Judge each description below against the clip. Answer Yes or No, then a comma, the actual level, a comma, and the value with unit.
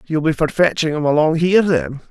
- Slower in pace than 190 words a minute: No, fast, 230 wpm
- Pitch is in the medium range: Yes, medium, 155 Hz